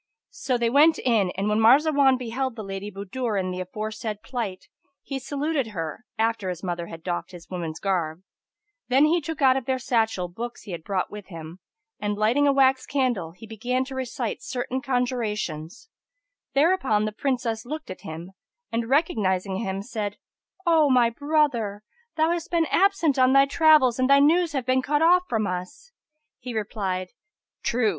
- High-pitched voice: Yes, high, 235 Hz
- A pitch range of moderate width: No, wide, 5.7 semitones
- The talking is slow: No, average, 175 wpm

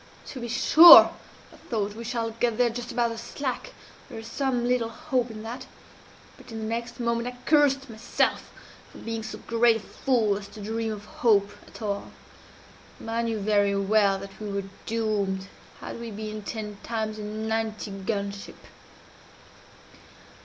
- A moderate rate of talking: Yes, average, 170 wpm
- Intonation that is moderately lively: No, narrow, 2.1 semitones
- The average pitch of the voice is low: No, high, 225 Hz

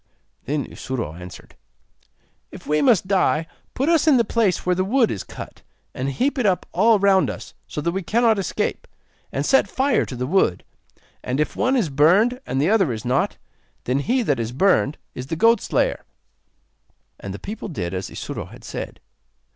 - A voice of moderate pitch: Yes, medium, 180 Hz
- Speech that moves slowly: No, average, 190 wpm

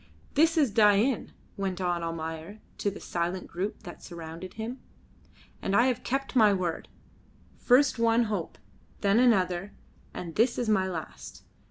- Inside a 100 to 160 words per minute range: Yes, average, 150 wpm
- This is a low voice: No, high, 200 Hz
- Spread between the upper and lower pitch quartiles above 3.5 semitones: Yes, average, 4.8 semitones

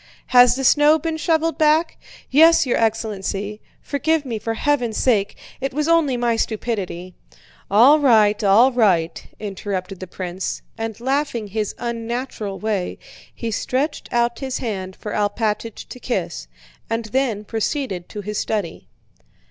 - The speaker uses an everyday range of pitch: Yes, average, 4.5 semitones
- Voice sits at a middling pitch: No, high, 225 Hz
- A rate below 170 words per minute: Yes, average, 140 wpm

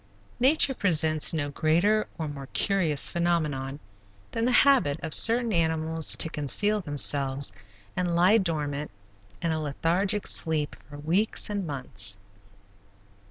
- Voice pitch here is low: No, medium, 160 Hz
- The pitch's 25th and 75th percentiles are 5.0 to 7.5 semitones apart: Yes, average, 5.3 semitones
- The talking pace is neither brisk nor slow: No, slow, 125 wpm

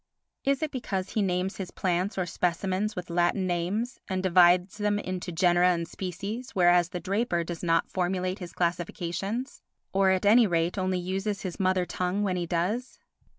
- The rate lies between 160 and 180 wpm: Yes, average, 175 wpm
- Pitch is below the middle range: No, medium, 185 Hz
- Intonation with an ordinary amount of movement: No, narrow, 2.2 semitones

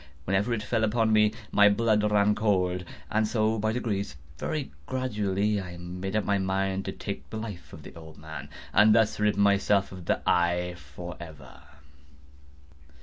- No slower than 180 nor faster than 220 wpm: No, average, 155 wpm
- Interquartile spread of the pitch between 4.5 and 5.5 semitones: No, average, 3.3 semitones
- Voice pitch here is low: Yes, low, 100 Hz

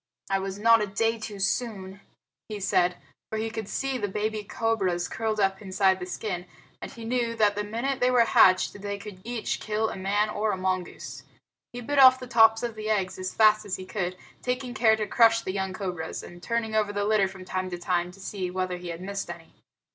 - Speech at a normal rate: No, fast, 225 wpm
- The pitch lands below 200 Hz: No, high, 205 Hz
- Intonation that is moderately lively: Yes, average, 3.1 semitones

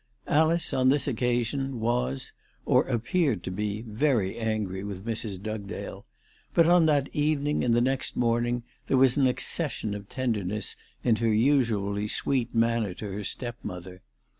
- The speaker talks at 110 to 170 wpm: Yes, average, 150 wpm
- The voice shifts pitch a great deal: No, average, 4.3 semitones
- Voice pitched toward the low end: Yes, low, 115 Hz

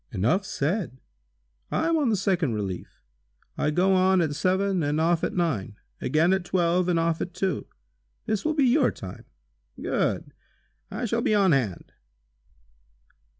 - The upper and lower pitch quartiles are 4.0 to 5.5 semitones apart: Yes, average, 4.3 semitones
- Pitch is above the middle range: No, medium, 180 Hz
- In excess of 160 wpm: No, average, 155 wpm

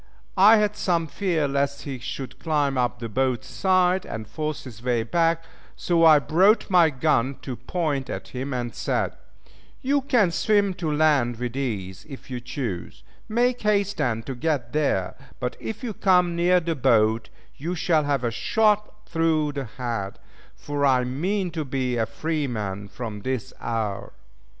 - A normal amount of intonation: No, wide, 6.2 semitones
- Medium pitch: Yes, medium, 145 Hz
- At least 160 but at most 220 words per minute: Yes, average, 170 wpm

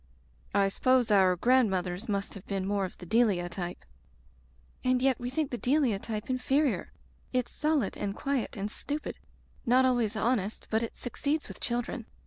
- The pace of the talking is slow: No, average, 170 wpm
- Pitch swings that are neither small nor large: Yes, average, 4.4 semitones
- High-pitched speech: Yes, high, 230 Hz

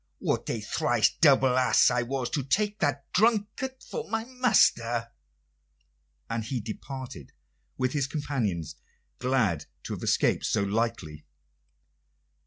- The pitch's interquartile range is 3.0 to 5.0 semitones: No, wide, 5.4 semitones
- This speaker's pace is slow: Yes, slow, 125 wpm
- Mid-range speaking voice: No, low, 130 Hz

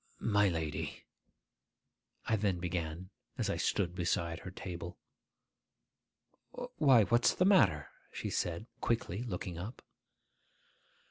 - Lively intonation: No, average, 4.3 semitones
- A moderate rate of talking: No, slow, 110 wpm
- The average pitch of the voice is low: Yes, very low, 95 Hz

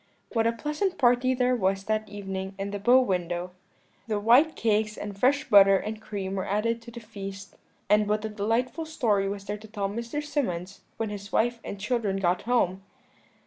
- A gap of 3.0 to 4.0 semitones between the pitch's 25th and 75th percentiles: Yes, average, 3.3 semitones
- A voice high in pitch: Yes, high, 210 Hz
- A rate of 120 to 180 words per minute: No, average, 195 wpm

